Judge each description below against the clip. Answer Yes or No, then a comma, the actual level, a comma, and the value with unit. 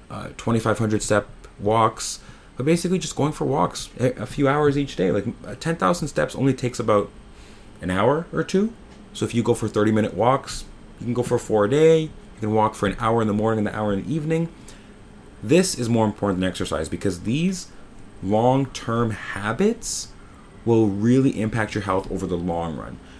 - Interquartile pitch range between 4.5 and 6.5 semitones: Yes, average, 5.1 semitones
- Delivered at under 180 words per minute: No, average, 195 wpm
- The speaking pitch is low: Yes, low, 110 Hz